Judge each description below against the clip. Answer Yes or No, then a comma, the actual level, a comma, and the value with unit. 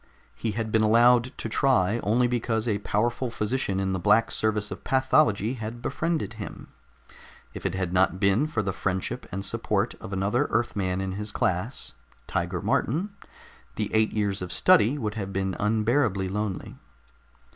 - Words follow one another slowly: No, average, 165 wpm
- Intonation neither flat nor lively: Yes, average, 3.5 semitones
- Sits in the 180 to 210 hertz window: No, low, 105 Hz